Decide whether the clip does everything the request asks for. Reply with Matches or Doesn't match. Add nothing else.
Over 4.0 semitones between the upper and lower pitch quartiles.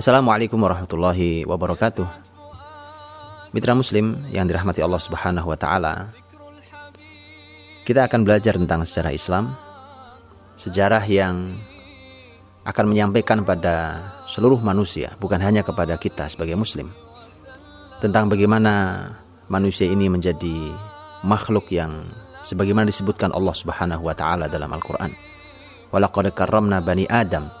Doesn't match